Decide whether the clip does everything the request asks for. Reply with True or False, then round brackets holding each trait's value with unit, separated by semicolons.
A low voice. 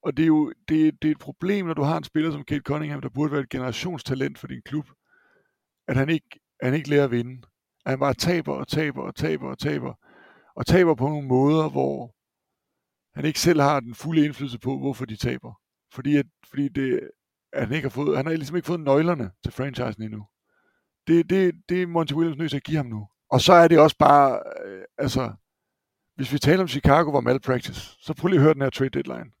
False (145 Hz)